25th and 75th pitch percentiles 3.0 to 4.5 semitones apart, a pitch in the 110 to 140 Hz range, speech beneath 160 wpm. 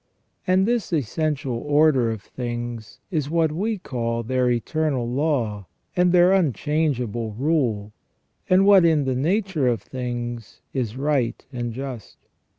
No: average, 5.2 semitones; low, 135 Hz; slow, 135 wpm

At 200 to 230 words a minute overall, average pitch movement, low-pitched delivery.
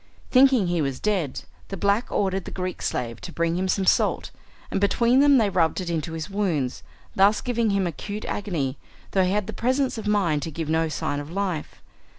No: fast, 205 wpm; average, 4.4 semitones; high, 190 Hz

